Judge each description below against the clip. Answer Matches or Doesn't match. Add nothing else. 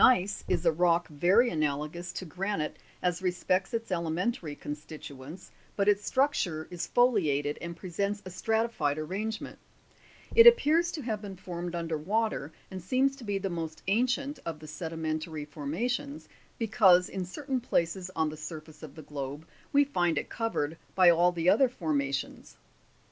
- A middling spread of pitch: Doesn't match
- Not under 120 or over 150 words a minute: Doesn't match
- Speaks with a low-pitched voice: Doesn't match